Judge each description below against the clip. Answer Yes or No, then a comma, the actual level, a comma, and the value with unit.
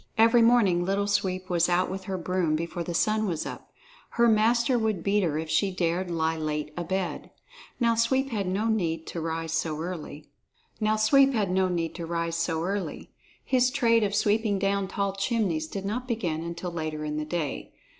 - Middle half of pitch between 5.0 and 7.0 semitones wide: No, average, 4.6 semitones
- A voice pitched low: No, medium, 185 Hz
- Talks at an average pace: Yes, average, 165 wpm